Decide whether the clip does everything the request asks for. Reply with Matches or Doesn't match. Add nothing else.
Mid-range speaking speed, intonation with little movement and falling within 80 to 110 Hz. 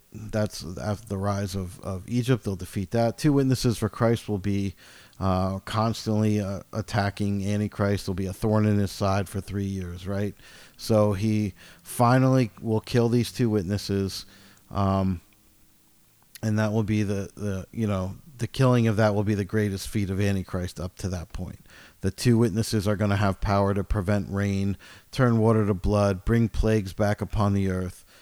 Matches